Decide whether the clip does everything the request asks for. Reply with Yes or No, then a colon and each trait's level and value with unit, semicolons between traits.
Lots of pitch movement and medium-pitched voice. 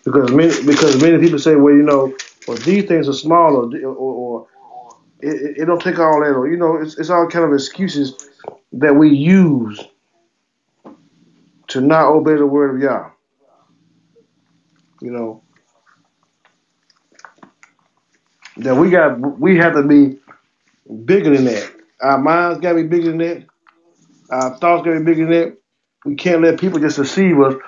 No: average, 3.3 semitones; medium, 155 Hz